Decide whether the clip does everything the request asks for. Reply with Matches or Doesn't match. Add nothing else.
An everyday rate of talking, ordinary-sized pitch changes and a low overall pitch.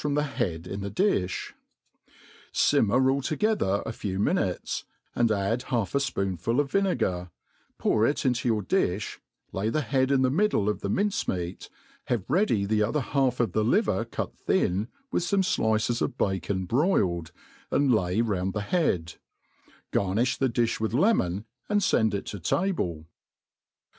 Doesn't match